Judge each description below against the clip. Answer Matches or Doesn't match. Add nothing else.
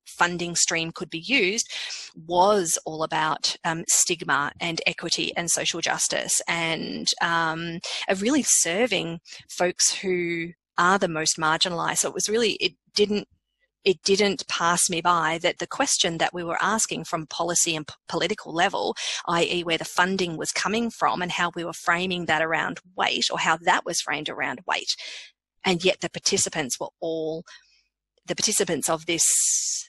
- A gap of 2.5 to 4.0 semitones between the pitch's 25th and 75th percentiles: Matches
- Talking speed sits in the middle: Matches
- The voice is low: Doesn't match